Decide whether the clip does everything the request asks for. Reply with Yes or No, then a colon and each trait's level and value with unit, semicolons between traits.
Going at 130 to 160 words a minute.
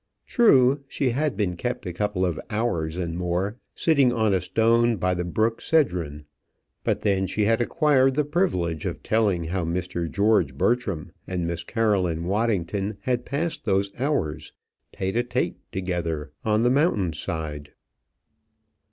Yes: average, 150 wpm